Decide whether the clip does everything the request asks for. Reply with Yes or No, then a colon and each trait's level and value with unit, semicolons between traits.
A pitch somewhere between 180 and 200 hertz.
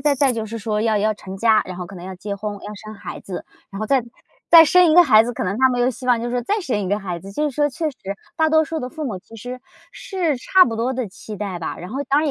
No: high, 230 Hz